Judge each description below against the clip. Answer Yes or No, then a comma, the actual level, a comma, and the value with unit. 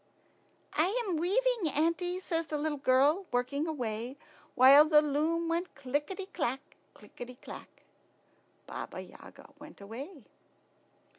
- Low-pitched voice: No, very high, 300 Hz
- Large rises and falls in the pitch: No, average, 4.3 semitones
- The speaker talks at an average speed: No, slow, 120 wpm